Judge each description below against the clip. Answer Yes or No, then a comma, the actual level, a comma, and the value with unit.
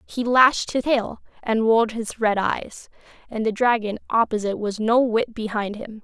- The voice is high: Yes, high, 225 Hz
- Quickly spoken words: No, average, 180 wpm